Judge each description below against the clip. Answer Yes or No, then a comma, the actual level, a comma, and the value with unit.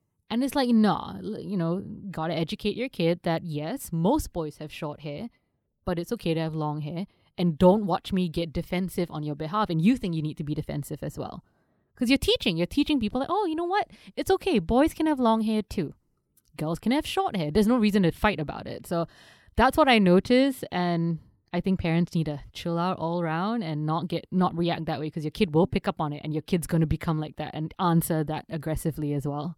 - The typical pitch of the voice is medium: Yes, medium, 175 Hz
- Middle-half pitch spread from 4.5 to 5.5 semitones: Yes, average, 5.2 semitones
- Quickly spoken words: Yes, fast, 245 wpm